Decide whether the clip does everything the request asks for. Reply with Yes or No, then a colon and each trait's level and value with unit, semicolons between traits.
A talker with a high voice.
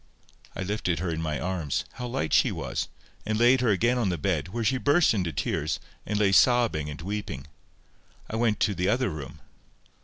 No: low, 100 Hz